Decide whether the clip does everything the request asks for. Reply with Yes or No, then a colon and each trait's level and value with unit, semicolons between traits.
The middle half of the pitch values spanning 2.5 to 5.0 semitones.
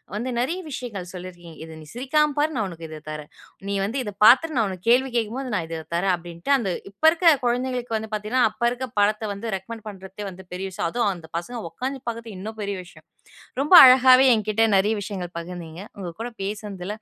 No: wide, 5.4 semitones